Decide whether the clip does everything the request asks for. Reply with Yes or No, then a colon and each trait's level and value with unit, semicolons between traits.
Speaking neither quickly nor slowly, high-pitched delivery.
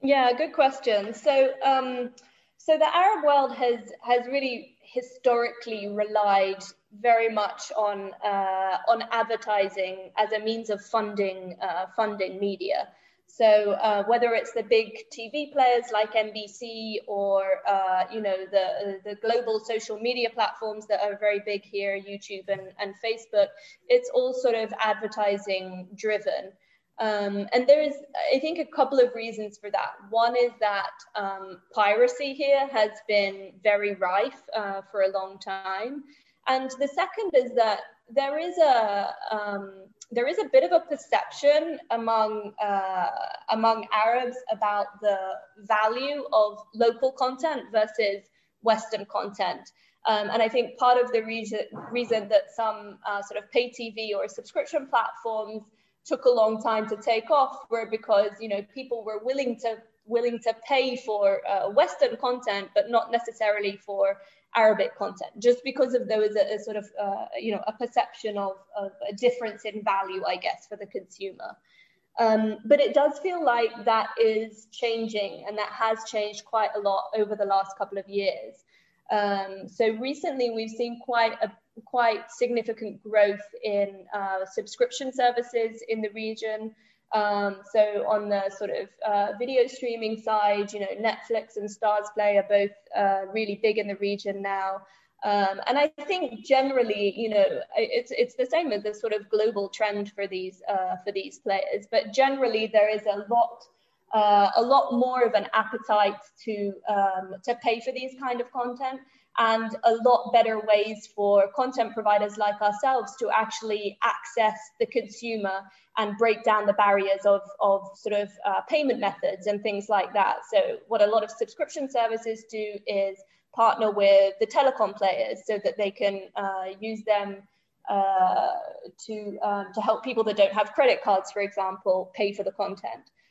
Yes: average, 165 wpm; high, 220 Hz